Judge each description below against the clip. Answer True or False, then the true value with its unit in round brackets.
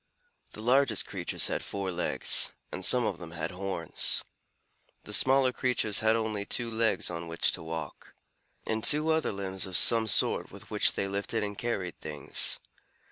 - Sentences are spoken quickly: False (170 wpm)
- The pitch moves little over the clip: False (4.1 semitones)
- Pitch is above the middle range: False (105 Hz)